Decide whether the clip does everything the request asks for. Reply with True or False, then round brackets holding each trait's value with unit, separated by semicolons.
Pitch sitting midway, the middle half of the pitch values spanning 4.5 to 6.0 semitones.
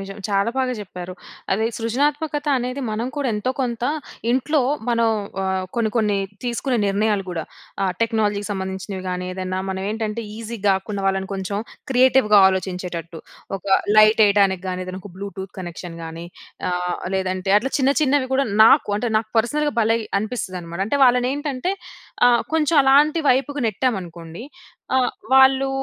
False (215 Hz; 5.1 semitones)